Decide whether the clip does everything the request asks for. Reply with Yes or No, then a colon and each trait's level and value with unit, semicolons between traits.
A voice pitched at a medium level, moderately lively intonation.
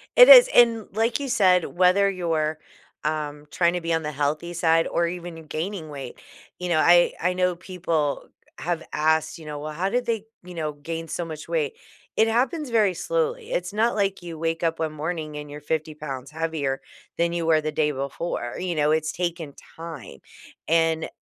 Yes: medium, 165 Hz; average, 3.1 semitones